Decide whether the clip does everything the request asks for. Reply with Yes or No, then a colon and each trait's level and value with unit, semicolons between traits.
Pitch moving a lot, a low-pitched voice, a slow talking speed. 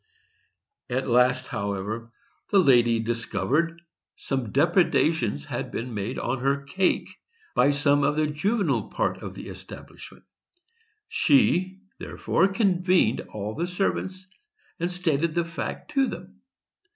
No: wide, 6.7 semitones; medium, 150 Hz; slow, 125 wpm